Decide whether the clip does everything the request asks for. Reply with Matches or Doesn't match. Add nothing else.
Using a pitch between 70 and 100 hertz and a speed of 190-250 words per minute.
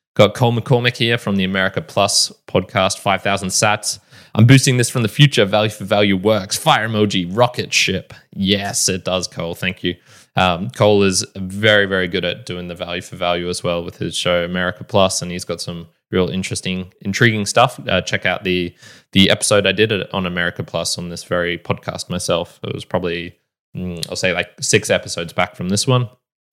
Matches